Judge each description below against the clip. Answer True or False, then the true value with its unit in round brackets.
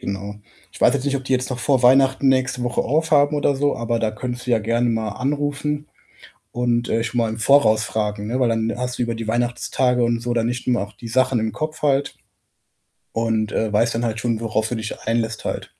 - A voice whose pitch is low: True (120 Hz)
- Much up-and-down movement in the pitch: False (2.7 semitones)